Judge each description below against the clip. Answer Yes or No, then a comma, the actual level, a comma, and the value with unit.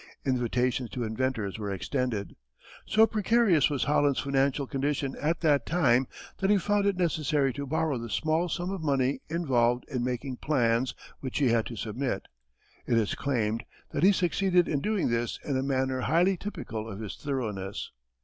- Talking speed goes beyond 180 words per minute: No, average, 170 wpm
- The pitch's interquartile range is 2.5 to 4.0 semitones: No, average, 5.0 semitones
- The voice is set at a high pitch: No, low, 135 Hz